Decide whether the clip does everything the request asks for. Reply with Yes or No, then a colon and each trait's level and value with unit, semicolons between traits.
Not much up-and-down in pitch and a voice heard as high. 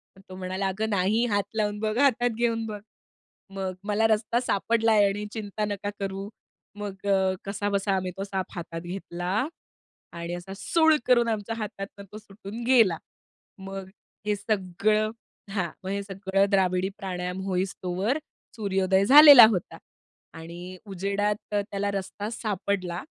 Yes: narrow, 2.2 semitones; high, 200 Hz